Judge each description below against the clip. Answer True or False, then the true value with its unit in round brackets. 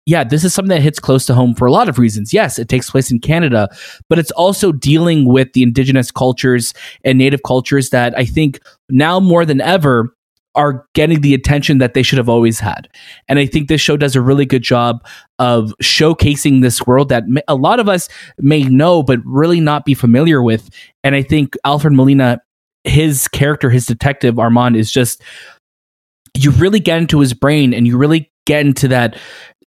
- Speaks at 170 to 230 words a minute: True (200 wpm)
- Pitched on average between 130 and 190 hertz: True (135 Hz)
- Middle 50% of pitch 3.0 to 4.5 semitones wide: True (3.3 semitones)